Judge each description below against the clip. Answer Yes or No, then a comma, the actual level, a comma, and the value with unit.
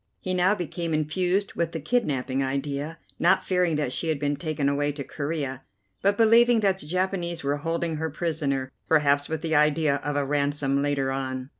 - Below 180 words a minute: No, average, 185 wpm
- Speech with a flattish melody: No, average, 3.4 semitones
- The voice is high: No, medium, 150 Hz